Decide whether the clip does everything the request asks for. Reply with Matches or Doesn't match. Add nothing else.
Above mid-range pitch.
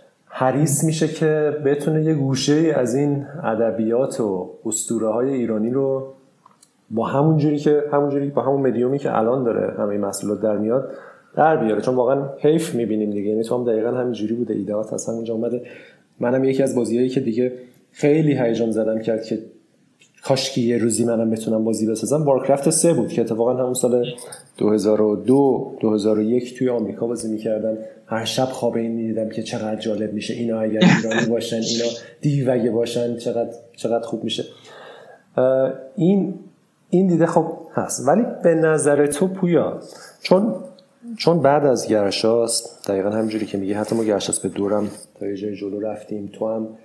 Doesn't match